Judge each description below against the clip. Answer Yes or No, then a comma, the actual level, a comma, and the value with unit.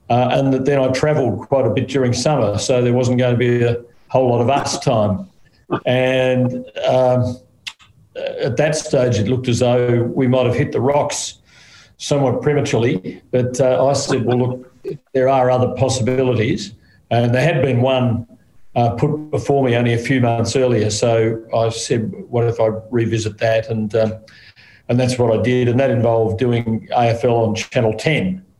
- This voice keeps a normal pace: Yes, average, 180 wpm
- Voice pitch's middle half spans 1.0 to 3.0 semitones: Yes, narrow, 2.4 semitones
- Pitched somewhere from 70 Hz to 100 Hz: No, low, 125 Hz